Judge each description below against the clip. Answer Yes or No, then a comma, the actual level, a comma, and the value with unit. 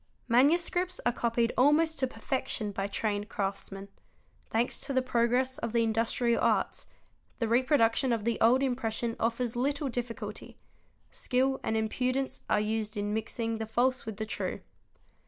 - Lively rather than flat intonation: No, average, 2.7 semitones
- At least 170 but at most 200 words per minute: No, average, 150 wpm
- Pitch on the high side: Yes, high, 235 Hz